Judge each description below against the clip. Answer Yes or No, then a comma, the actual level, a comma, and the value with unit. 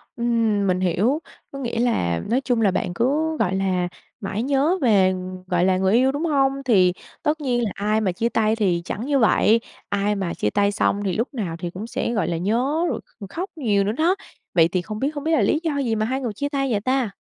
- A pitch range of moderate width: No, wide, 5.7 semitones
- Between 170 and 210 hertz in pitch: No, high, 225 Hz